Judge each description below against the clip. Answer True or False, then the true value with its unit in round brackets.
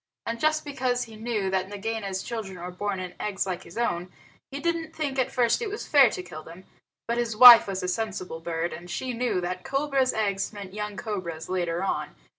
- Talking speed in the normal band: False (220 wpm)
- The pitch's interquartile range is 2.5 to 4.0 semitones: False (5.1 semitones)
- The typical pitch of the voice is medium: False (210 Hz)